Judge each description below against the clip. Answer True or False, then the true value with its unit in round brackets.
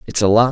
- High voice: False (115 Hz)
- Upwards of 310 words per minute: True (345 wpm)